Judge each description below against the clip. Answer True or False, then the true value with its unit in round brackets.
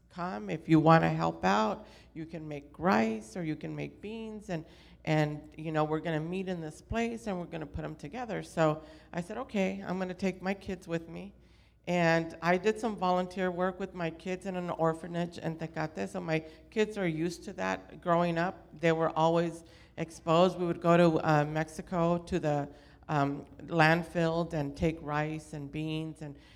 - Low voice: False (165 Hz)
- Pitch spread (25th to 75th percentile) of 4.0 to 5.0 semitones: False (2.6 semitones)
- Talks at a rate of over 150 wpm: True (200 wpm)